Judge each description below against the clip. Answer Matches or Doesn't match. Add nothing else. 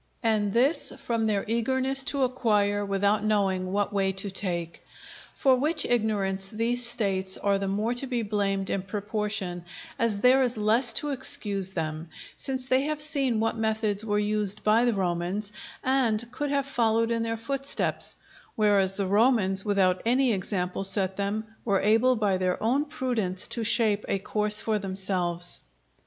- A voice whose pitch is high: Matches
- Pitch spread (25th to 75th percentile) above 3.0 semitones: Matches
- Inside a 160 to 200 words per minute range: Matches